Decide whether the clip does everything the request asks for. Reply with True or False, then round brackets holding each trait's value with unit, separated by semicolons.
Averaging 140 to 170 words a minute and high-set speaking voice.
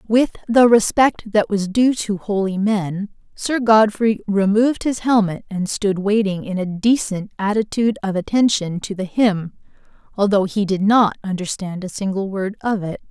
True (165 wpm; 205 Hz)